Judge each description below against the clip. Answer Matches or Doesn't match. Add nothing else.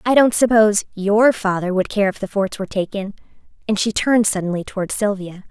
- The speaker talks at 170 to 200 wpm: Matches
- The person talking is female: Matches